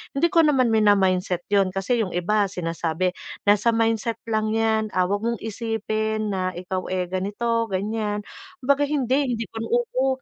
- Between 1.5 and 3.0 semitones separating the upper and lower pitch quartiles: No, average, 3.6 semitones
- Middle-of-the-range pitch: No, high, 215 Hz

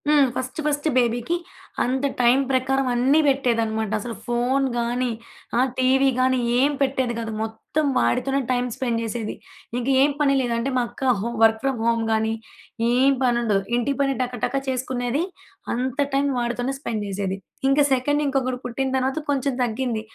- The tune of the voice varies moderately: No, narrow, 2.3 semitones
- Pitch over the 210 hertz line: Yes, very high, 255 Hz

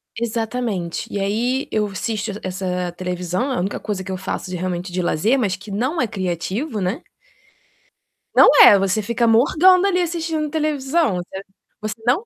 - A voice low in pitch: No, high, 215 Hz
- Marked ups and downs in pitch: Yes, wide, 6.1 semitones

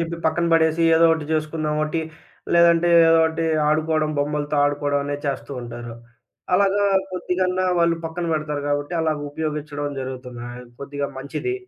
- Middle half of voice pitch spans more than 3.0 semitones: No, narrow, 2.5 semitones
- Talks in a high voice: No, medium, 155 Hz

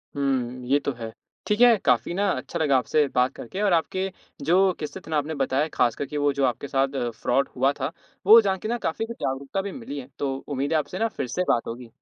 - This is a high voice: No, medium, 145 Hz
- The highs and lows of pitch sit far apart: Yes, wide, 6.1 semitones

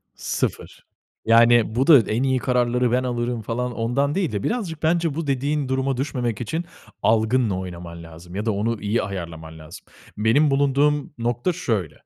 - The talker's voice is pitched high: No, low, 120 Hz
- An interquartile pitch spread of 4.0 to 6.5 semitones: Yes, average, 4.7 semitones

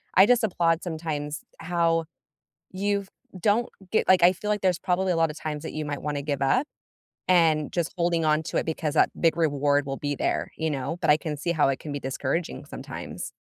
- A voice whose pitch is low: No, medium, 160 Hz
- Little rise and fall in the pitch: No, average, 3.1 semitones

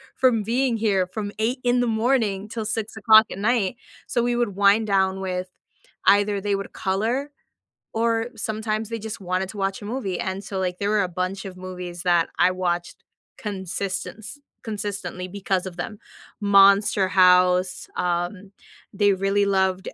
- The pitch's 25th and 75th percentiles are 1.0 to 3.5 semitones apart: Yes, average, 2.7 semitones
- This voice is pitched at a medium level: No, high, 200 Hz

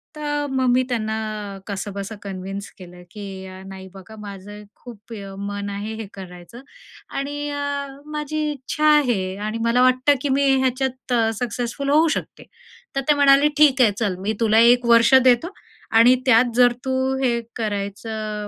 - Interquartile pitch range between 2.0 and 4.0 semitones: No, average, 4.8 semitones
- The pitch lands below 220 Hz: No, high, 235 Hz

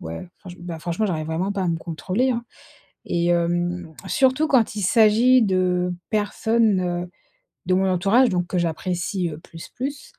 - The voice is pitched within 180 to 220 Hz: Yes, medium, 185 Hz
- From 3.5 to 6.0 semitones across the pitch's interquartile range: Yes, average, 4.0 semitones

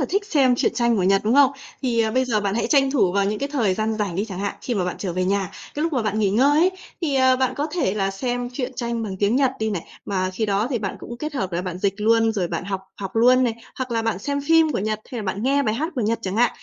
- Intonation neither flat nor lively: Yes, average, 4.6 semitones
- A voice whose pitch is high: Yes, high, 225 Hz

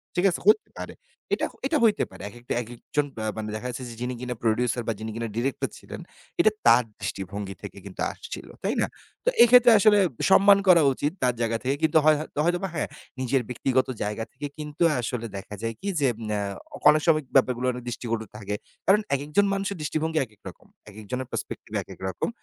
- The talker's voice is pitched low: Yes, low, 125 Hz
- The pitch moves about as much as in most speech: No, wide, 5.9 semitones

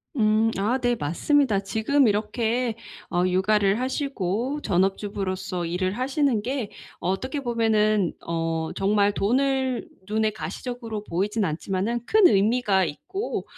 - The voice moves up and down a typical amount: Yes, average, 4.4 semitones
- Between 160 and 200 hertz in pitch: No, high, 215 Hz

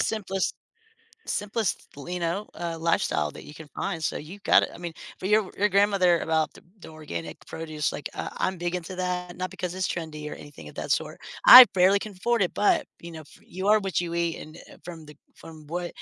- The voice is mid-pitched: Yes, medium, 175 Hz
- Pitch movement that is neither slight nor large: Yes, average, 3.2 semitones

